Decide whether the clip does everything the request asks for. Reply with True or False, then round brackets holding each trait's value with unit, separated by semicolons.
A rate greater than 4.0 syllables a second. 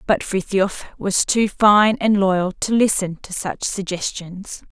False (3.7 syllables/s)